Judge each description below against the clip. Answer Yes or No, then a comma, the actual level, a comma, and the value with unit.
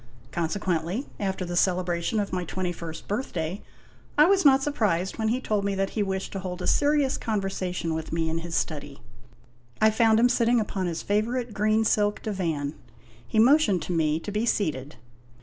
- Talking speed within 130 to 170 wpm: No, average, 185 wpm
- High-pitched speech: Yes, high, 195 Hz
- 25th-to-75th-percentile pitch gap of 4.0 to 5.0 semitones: Yes, average, 4.5 semitones